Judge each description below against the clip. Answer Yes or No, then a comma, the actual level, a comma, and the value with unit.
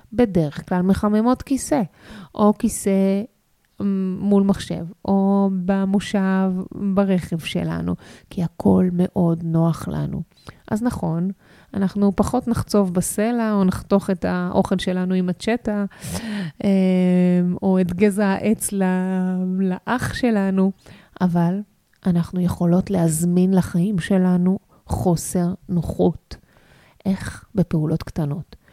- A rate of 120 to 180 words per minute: No, slow, 100 wpm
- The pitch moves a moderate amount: No, narrow, 2.1 semitones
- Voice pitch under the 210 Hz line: Yes, high, 190 Hz